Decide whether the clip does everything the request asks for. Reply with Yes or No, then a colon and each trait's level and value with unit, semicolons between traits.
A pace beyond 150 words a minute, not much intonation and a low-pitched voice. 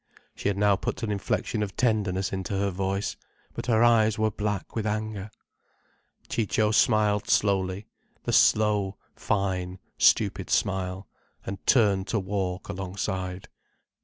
No: slow, 135 wpm; narrow, 2.1 semitones; low, 100 Hz